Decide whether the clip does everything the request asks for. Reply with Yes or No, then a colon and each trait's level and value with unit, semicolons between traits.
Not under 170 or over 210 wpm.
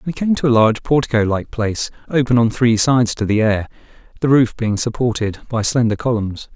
Yes: average, 200 wpm